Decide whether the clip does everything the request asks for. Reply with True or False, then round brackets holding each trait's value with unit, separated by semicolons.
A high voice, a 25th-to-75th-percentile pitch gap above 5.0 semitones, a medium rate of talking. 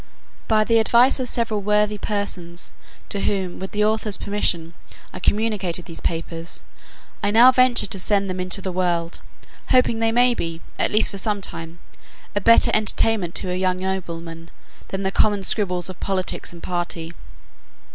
False (195 Hz; 3.5 semitones; 165 wpm)